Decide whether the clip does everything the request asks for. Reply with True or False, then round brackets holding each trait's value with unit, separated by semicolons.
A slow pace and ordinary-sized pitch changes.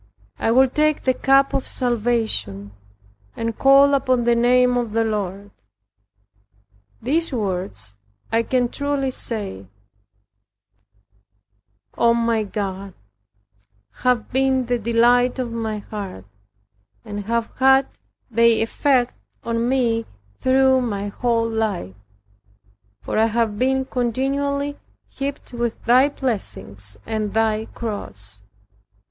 True (110 wpm; 3.4 semitones)